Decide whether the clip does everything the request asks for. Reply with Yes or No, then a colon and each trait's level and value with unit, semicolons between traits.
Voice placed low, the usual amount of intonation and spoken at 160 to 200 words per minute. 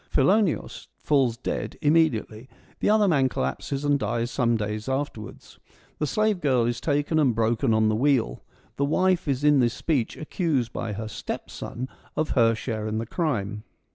Yes: low, 130 Hz; average, 4.8 semitones; average, 170 wpm